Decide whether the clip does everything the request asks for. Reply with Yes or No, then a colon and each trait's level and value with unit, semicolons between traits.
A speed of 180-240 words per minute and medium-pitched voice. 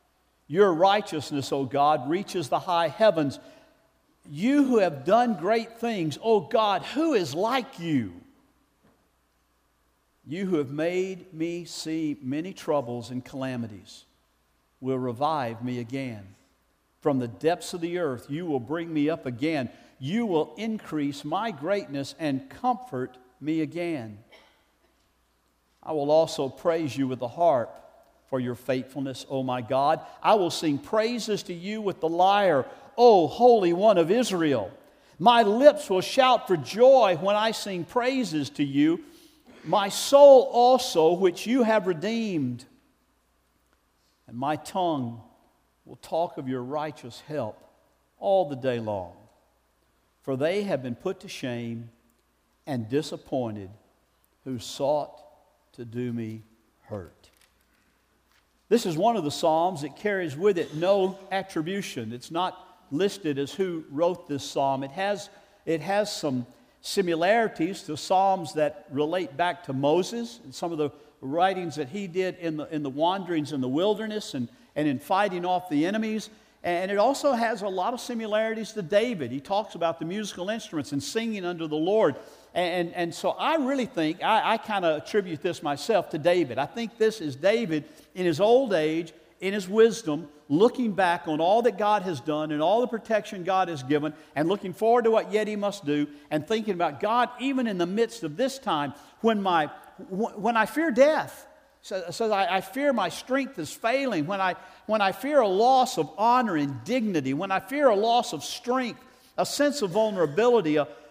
No: average, 170 wpm; medium, 175 Hz